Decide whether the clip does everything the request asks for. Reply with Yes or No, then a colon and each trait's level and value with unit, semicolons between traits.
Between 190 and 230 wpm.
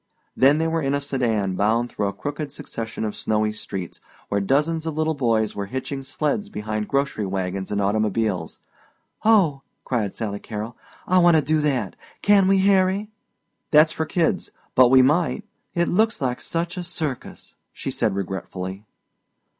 No: average, 170 wpm